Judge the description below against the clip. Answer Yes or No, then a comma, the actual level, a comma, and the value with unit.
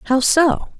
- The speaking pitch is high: Yes, very high, 290 Hz